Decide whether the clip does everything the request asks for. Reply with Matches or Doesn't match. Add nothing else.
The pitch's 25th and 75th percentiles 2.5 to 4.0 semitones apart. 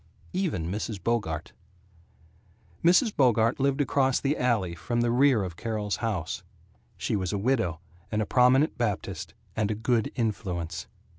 Doesn't match